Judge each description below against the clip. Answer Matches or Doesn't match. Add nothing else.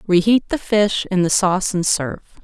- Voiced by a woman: Matches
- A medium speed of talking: Matches